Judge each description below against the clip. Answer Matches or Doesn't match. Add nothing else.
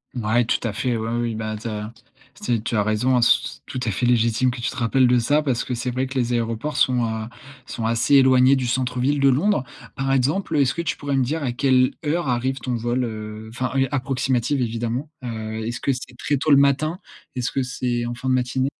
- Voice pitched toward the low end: Matches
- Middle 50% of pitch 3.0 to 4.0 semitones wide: Doesn't match